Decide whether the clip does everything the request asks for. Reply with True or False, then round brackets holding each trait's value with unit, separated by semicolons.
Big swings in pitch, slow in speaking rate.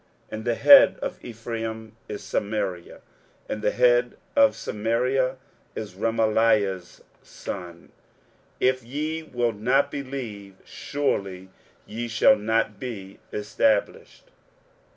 False (3.4 semitones; 110 wpm)